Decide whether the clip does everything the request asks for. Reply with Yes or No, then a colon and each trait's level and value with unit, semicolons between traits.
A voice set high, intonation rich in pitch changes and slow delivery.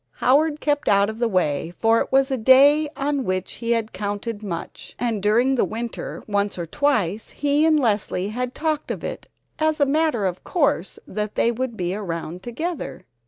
No: high, 230 Hz; wide, 5.9 semitones; average, 190 wpm